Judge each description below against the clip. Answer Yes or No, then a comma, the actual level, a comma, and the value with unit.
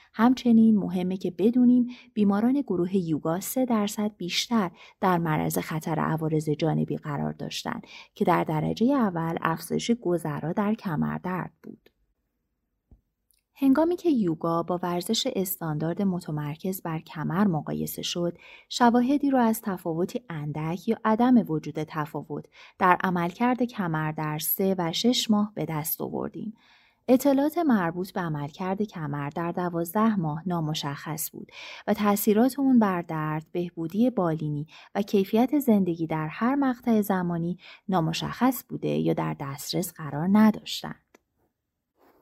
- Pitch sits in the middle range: Yes, medium, 180 Hz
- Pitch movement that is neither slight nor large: No, wide, 6.0 semitones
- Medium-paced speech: Yes, average, 125 wpm